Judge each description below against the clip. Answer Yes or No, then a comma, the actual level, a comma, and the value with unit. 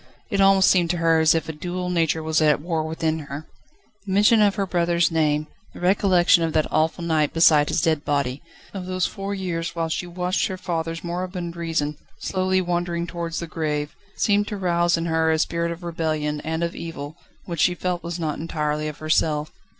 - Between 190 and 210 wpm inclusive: Yes, fast, 205 wpm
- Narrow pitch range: Yes, narrow, 2.2 semitones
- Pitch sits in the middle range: Yes, medium, 170 Hz